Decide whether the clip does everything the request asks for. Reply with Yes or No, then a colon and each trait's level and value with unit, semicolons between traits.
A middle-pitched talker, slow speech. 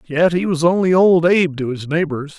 No: medium, 165 Hz; fast, 225 wpm